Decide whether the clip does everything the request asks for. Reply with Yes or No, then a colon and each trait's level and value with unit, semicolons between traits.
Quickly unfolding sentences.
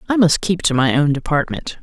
Yes: fast, 230 wpm